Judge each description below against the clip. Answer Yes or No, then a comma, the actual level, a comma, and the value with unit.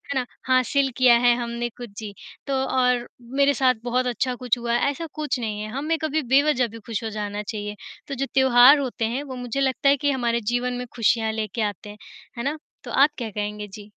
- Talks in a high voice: Yes, high, 245 Hz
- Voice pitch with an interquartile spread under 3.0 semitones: No, average, 3.3 semitones